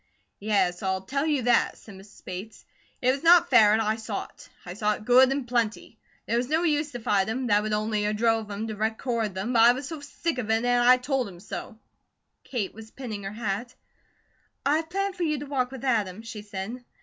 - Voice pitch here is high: Yes, high, 225 Hz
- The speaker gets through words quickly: Yes, fast, 230 wpm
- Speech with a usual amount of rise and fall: Yes, average, 3.5 semitones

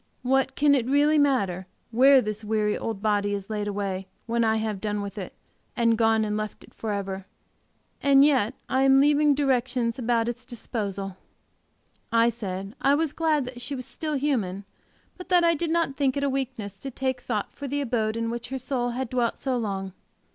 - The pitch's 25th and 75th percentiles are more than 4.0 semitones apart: Yes, average, 4.6 semitones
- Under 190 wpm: No, average, 200 wpm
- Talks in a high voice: Yes, high, 235 Hz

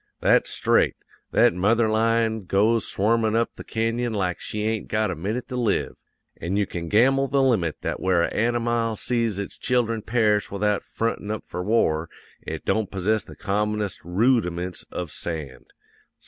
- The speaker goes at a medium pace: Yes, average, 165 wpm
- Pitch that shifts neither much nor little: Yes, average, 3.4 semitones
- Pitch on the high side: No, low, 110 Hz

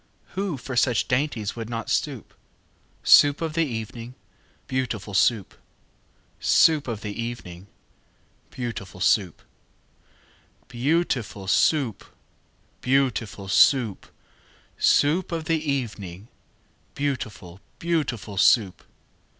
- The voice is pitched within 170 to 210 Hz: No, low, 120 Hz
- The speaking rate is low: Yes, slow, 115 wpm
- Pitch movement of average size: No, wide, 5.7 semitones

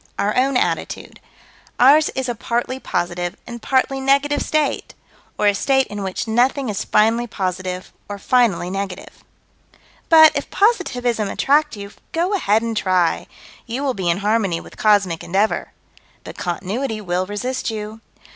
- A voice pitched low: No, high, 220 Hz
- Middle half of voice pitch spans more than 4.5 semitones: Yes, average, 5.3 semitones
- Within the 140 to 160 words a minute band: Yes, average, 150 wpm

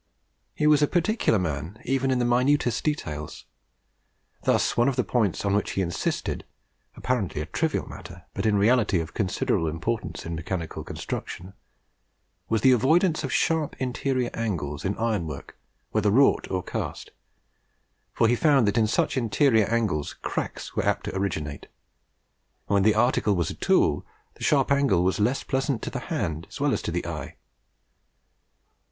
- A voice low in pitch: Yes, low, 110 Hz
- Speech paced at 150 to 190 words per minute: Yes, average, 160 wpm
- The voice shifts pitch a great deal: Yes, wide, 6.4 semitones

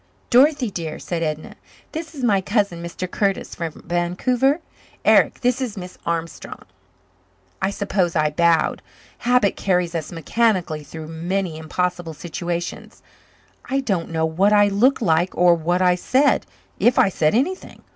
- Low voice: No, medium, 180 Hz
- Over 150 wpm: No, average, 145 wpm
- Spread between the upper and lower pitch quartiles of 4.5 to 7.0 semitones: Yes, average, 5.0 semitones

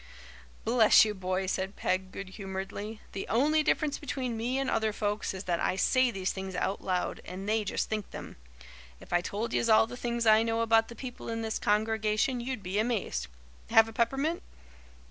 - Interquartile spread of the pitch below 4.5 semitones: Yes, average, 3.4 semitones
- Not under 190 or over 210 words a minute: Yes, average, 195 wpm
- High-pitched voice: Yes, high, 220 Hz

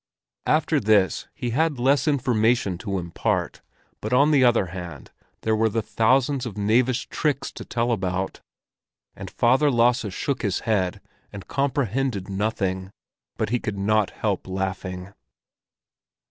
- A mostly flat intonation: No, average, 4.9 semitones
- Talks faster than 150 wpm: No, average, 140 wpm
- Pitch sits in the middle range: No, low, 110 Hz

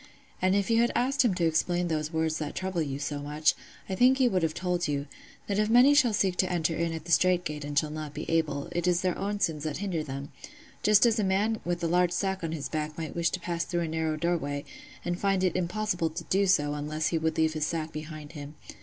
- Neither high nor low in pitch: Yes, medium, 170 Hz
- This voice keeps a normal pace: No, fast, 260 wpm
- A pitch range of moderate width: Yes, average, 3.4 semitones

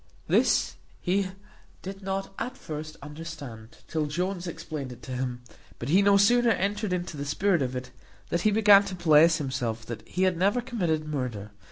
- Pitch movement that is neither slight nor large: No, wide, 6.0 semitones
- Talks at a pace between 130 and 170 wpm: No, average, 180 wpm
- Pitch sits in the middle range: Yes, medium, 165 Hz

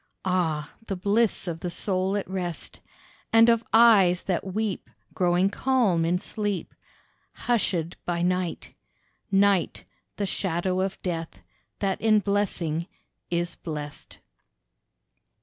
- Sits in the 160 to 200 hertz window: Yes, medium, 185 Hz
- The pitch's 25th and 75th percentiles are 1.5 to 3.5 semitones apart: Yes, average, 2.8 semitones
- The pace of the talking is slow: Yes, slow, 115 wpm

